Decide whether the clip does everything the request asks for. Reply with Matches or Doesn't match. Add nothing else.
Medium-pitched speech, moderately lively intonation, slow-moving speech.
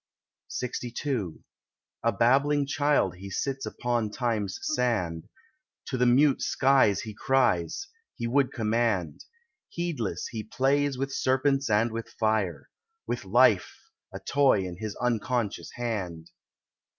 Doesn't match